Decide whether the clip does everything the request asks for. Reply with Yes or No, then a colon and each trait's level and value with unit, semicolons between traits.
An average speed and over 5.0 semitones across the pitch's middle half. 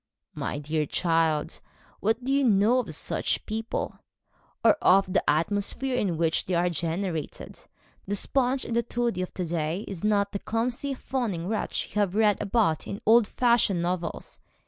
Yes: average, 165 wpm; wide, 5.4 semitones